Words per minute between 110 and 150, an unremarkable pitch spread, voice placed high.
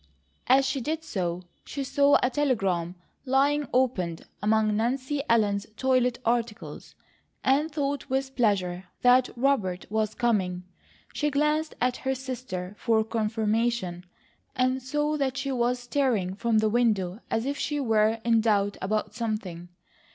Yes: average, 140 wpm; average, 4.1 semitones; high, 235 Hz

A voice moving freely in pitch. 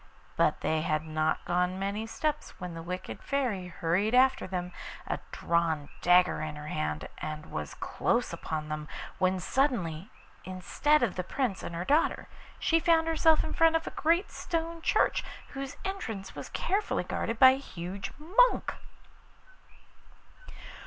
Yes: wide, 8.9 semitones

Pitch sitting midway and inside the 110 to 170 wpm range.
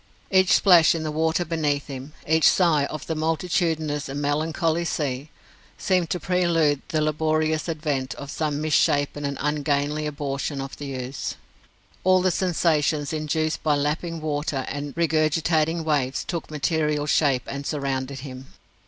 Yes: medium, 155 Hz; average, 150 wpm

